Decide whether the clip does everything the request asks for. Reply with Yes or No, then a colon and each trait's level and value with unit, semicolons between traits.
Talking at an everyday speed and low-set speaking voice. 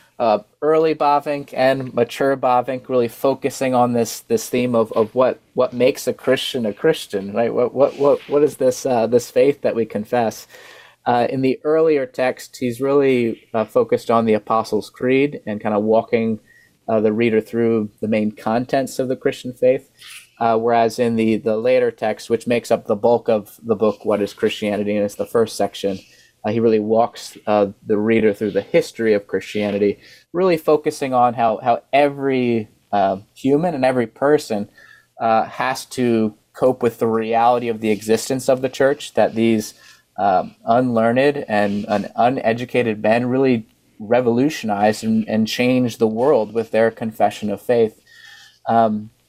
Yes: average, 175 wpm; low, 120 Hz